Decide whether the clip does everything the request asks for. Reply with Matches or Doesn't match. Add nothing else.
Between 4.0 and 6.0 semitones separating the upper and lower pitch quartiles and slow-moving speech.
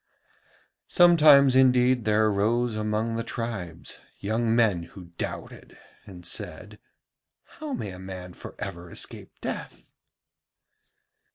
Matches